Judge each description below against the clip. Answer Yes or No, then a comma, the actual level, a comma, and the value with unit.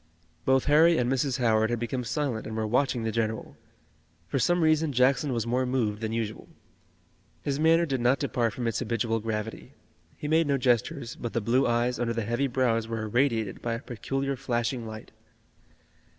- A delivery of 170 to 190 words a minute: Yes, average, 185 wpm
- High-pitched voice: No, low, 120 Hz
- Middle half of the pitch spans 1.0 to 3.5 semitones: Yes, average, 3.1 semitones